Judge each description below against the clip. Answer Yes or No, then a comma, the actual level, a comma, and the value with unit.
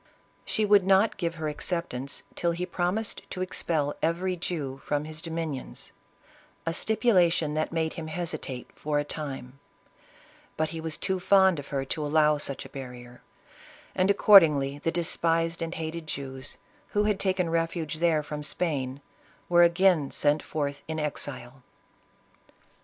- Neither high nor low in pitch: Yes, medium, 160 Hz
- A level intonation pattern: No, average, 3.2 semitones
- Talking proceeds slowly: No, average, 150 wpm